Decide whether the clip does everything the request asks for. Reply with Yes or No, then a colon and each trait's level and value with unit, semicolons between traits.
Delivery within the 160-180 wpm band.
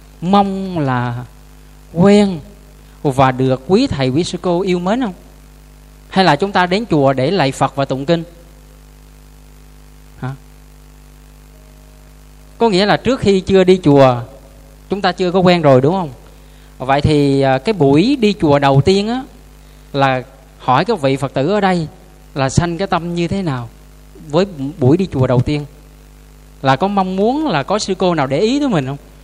Yes: average, 175 wpm